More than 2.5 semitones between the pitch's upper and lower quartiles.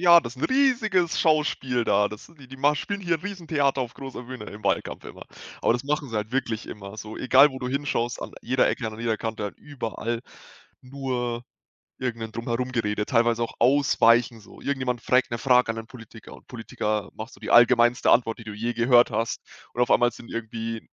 Yes: average, 2.9 semitones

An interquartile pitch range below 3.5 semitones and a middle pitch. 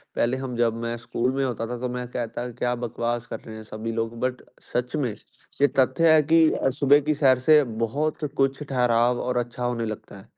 No: narrow, 2.6 semitones; low, 125 Hz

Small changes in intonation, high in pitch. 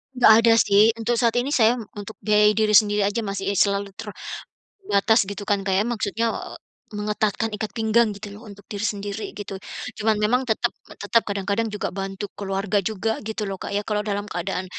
Yes: narrow, 1.7 semitones; high, 210 Hz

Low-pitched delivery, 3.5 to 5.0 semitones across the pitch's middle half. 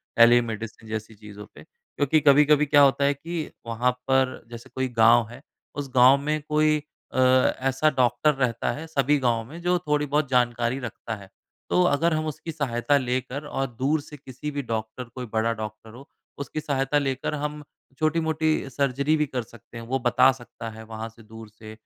Yes: low, 130 Hz; average, 4.1 semitones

